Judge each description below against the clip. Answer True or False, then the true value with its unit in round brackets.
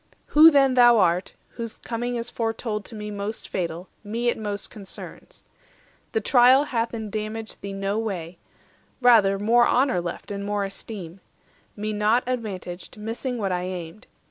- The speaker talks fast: False (155 wpm)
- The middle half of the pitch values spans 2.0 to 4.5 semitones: True (3.3 semitones)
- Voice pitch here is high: True (215 Hz)